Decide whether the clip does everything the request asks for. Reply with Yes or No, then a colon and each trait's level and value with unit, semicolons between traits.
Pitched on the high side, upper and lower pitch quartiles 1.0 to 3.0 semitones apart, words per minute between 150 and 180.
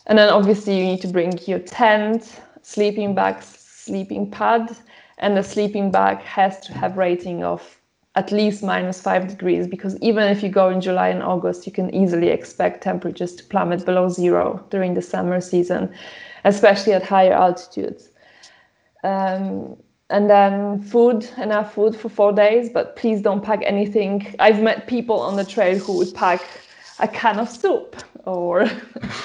Yes: high, 195 Hz; average, 2.7 semitones; average, 165 wpm